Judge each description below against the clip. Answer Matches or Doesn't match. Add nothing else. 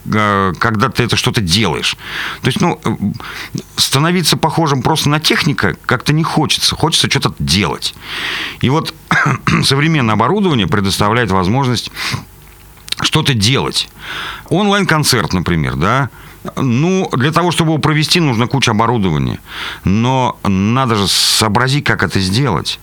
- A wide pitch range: Matches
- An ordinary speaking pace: Matches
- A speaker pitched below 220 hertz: Matches